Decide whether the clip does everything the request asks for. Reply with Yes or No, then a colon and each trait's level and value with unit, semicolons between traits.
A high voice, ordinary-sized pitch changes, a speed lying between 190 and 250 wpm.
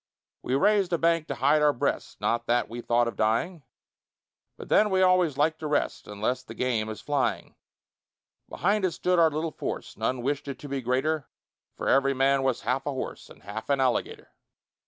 No: medium, 140 Hz; average, 4.5 semitones; average, 200 wpm